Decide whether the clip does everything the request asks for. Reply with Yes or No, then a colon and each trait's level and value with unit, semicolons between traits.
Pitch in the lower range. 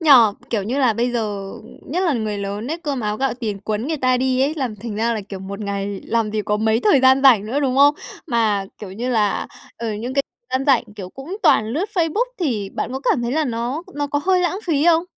No: high, 240 Hz